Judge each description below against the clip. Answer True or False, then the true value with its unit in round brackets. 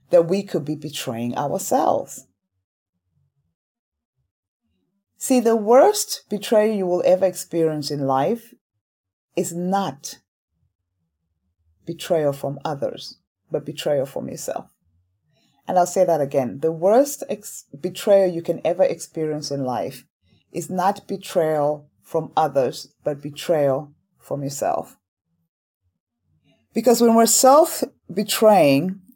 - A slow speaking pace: True (110 wpm)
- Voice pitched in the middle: True (150 Hz)